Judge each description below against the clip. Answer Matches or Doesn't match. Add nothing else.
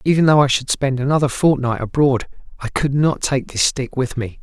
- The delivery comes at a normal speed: Doesn't match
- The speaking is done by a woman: Doesn't match